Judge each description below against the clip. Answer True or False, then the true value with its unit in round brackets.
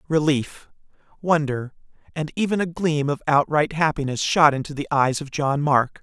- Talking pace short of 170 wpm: True (160 wpm)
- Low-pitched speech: False (150 Hz)